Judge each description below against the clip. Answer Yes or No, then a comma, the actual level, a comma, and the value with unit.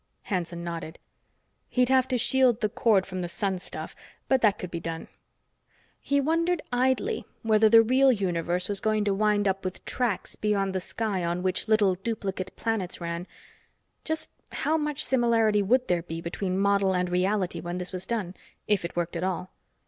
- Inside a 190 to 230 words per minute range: No, average, 180 wpm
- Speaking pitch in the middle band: No, high, 200 Hz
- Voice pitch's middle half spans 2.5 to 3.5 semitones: No, average, 4.3 semitones